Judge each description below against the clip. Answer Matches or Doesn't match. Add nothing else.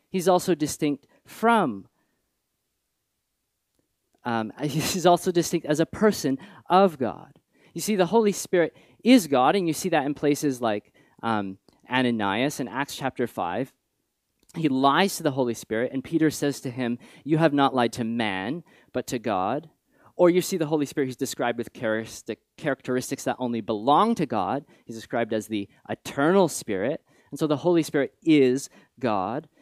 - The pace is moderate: Matches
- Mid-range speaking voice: Matches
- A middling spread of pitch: Doesn't match